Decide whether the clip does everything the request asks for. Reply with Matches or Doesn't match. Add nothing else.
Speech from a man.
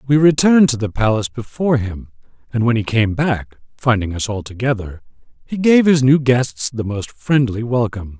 Matches